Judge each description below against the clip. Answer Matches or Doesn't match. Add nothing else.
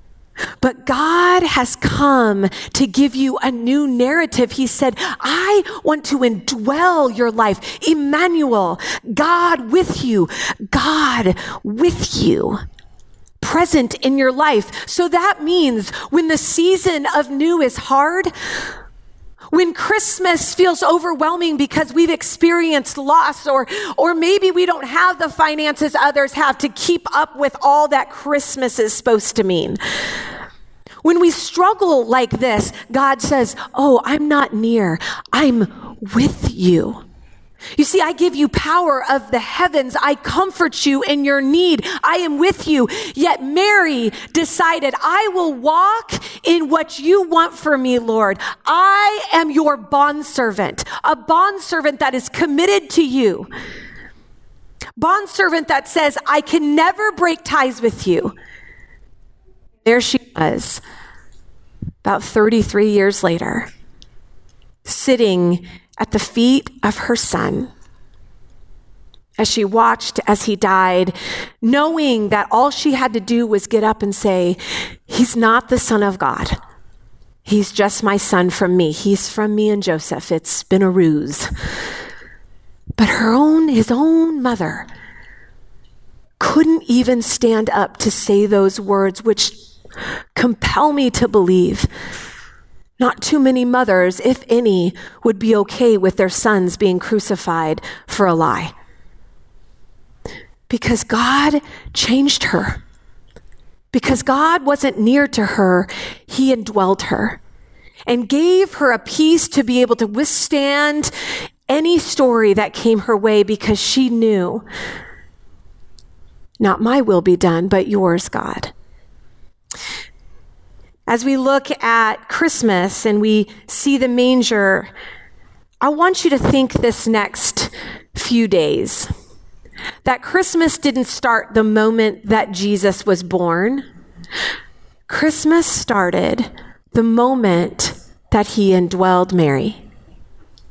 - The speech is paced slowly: Matches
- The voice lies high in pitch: Matches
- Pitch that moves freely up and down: Matches